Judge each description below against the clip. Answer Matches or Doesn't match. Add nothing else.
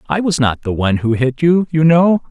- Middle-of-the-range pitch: Matches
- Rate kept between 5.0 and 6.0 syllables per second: Matches